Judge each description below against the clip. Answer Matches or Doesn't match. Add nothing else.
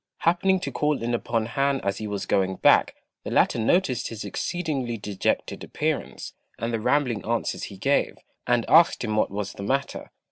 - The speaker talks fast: Doesn't match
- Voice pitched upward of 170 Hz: Doesn't match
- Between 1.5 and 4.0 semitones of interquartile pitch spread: Doesn't match